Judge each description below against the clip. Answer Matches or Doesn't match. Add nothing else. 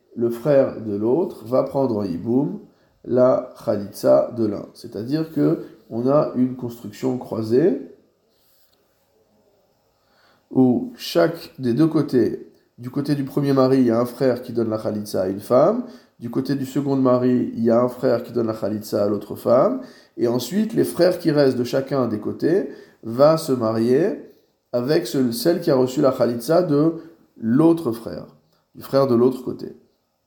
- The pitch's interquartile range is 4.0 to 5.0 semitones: Doesn't match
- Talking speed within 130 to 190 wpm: Matches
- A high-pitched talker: Doesn't match